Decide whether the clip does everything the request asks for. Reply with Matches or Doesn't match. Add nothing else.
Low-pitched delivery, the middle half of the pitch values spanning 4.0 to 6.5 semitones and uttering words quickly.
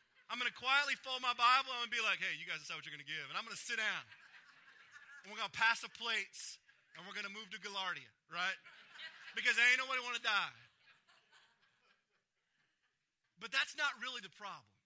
Doesn't match